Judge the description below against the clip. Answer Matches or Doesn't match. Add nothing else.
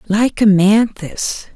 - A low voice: Doesn't match